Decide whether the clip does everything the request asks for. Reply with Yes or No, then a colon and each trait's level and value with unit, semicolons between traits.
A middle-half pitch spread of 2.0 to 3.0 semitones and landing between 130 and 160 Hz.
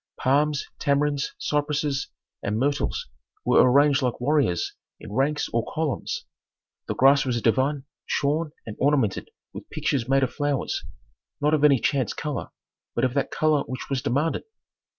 Yes: narrow, 2.4 semitones; medium, 140 Hz